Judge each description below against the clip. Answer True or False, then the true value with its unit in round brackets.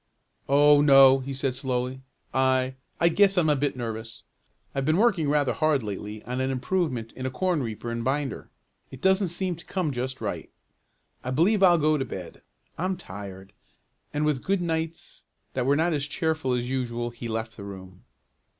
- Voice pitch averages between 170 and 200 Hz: False (135 Hz)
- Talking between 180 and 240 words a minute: True (185 wpm)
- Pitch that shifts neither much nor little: True (4.7 semitones)